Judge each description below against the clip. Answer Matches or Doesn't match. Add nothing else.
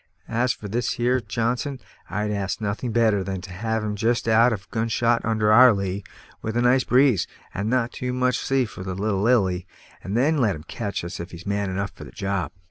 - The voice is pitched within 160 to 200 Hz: Doesn't match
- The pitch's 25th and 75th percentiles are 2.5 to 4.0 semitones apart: Matches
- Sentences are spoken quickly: Matches